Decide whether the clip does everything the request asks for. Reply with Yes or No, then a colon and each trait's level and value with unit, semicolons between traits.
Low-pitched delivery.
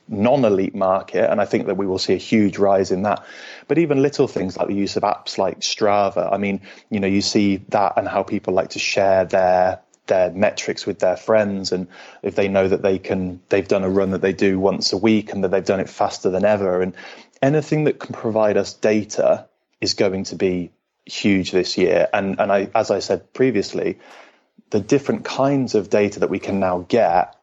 Yes: low, 100 Hz